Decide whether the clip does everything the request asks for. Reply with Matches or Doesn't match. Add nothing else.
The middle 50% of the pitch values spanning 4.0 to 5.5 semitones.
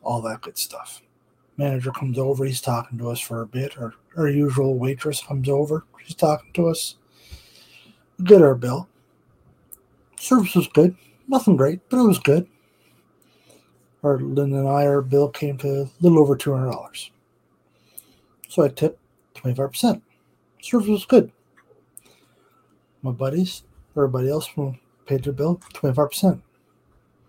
Doesn't match